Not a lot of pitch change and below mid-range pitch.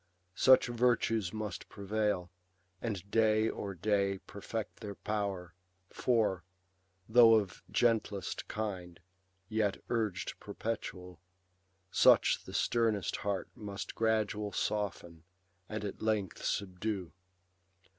Yes: narrow, 2.3 semitones; low, 105 Hz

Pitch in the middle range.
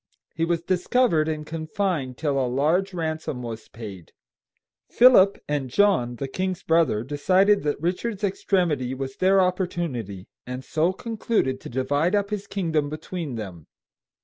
Yes: medium, 160 Hz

